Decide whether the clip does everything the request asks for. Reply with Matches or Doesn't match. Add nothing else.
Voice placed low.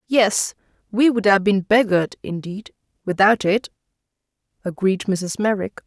Doesn't match